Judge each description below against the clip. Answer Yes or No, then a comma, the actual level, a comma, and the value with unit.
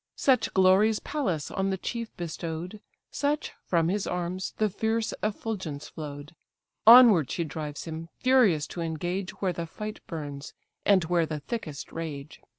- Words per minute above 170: No, average, 150 wpm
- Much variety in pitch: No, average, 5.0 semitones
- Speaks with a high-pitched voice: No, medium, 180 Hz